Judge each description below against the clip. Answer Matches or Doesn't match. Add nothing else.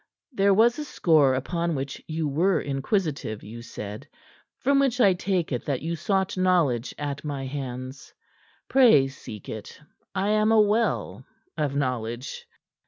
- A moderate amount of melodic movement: Doesn't match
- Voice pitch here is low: Doesn't match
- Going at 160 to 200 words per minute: Doesn't match